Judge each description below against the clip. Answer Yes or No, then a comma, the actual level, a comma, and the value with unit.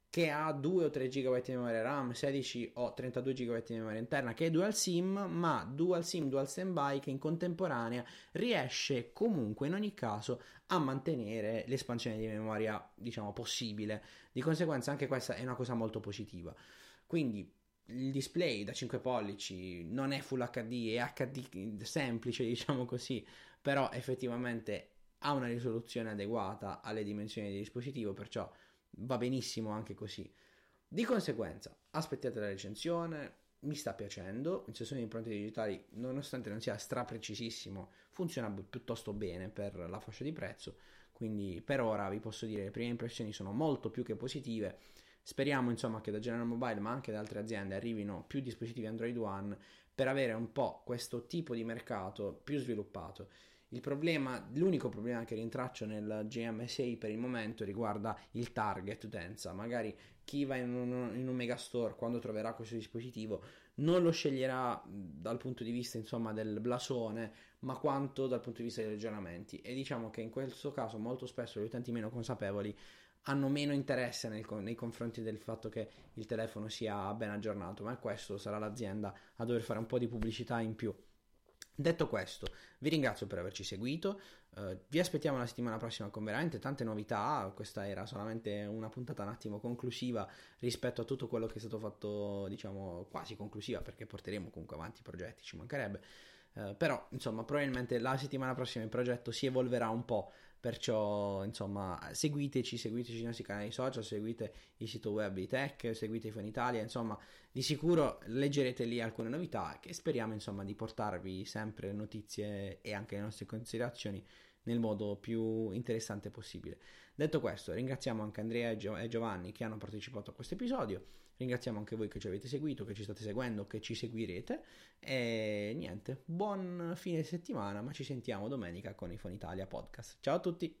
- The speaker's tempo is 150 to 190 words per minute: Yes, fast, 170 wpm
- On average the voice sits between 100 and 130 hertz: Yes, low, 115 Hz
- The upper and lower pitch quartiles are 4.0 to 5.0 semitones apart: No, average, 3.4 semitones